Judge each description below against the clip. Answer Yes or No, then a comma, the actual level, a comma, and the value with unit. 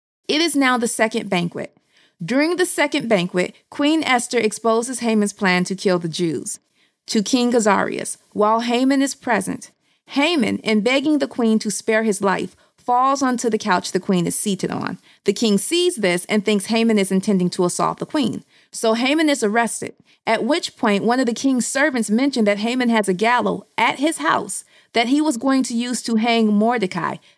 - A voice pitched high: Yes, high, 230 Hz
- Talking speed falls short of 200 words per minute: Yes, average, 190 wpm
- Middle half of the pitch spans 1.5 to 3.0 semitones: No, average, 4.2 semitones